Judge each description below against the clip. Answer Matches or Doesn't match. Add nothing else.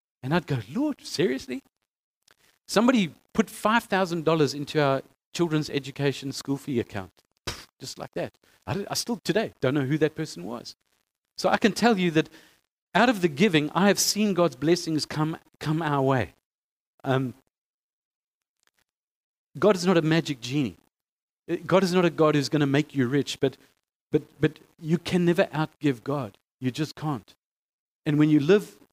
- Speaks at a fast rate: Doesn't match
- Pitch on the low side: Doesn't match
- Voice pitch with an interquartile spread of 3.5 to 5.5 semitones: Matches